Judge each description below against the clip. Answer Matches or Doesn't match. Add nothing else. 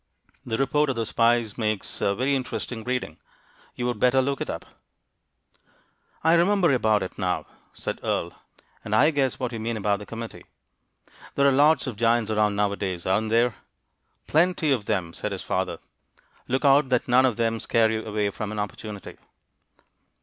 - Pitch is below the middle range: Matches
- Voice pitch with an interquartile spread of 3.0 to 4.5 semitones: Matches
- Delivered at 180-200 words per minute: Doesn't match